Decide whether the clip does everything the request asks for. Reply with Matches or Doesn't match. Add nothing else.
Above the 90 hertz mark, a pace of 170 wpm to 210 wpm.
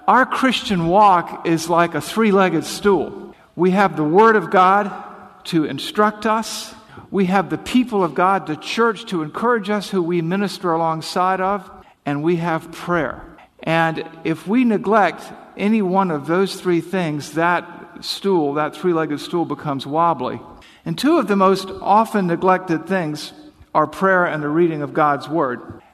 Doesn't match